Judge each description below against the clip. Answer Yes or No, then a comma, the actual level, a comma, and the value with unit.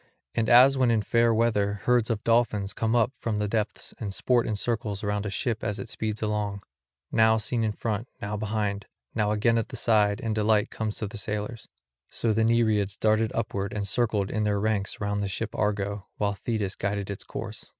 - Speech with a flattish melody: Yes, narrow, 1.8 semitones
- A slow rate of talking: No, fast, 205 wpm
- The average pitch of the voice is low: Yes, low, 105 Hz